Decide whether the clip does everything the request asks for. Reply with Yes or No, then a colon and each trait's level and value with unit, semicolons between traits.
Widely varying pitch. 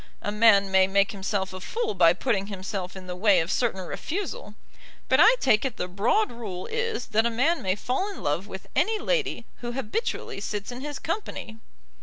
Yes: wide, 6.3 semitones